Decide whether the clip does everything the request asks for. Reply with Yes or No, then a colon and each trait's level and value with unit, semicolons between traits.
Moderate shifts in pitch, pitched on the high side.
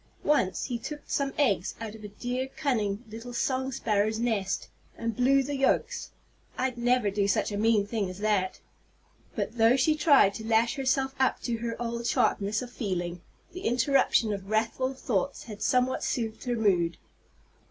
Yes: average, 3.8 semitones; high, 230 Hz